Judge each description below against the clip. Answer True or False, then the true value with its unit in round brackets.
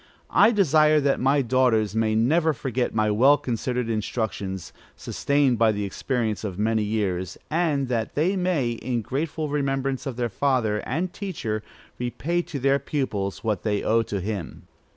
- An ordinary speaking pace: True (160 wpm)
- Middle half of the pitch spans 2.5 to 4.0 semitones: False (4.7 semitones)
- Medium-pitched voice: False (125 Hz)